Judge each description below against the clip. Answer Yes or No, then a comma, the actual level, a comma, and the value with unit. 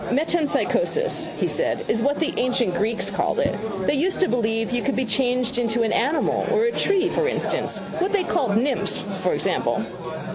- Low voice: No, very high, 255 Hz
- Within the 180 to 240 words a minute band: Yes, average, 185 wpm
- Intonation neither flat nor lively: No, wide, 7.3 semitones